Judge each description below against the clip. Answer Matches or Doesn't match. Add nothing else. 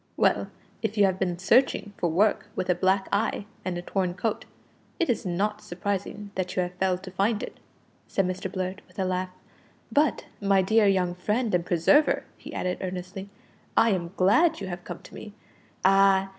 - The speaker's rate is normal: Matches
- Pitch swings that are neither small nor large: Doesn't match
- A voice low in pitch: Doesn't match